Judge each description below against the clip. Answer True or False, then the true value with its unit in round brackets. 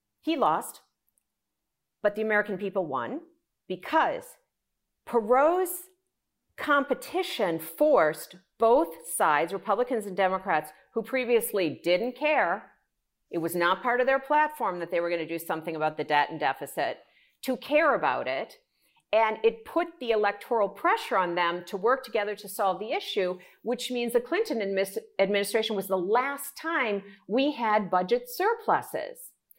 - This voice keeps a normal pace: True (145 wpm)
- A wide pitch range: True (6.9 semitones)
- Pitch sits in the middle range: False (220 Hz)